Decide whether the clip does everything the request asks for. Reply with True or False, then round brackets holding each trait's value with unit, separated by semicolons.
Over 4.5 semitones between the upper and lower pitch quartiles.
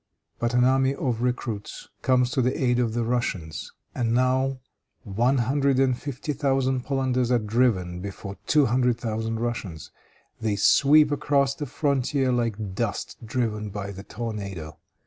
False (3.4 semitones)